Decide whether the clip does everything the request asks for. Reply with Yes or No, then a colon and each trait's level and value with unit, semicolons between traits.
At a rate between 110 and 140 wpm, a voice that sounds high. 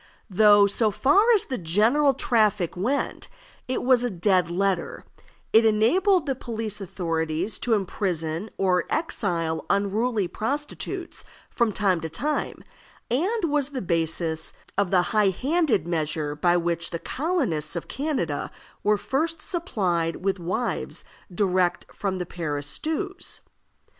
Yes: slow, 135 wpm; high, 200 Hz